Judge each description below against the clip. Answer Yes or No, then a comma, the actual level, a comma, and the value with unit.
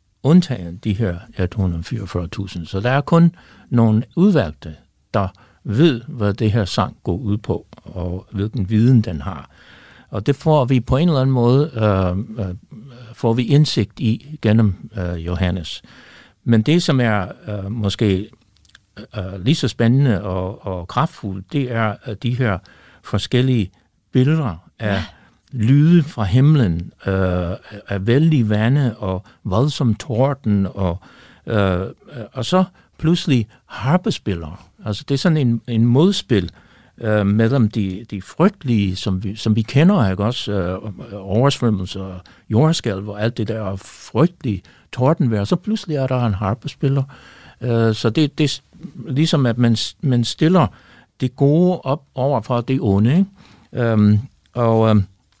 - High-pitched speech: No, low, 115 Hz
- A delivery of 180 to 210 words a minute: No, slow, 145 wpm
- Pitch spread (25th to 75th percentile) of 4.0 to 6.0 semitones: Yes, wide, 5.4 semitones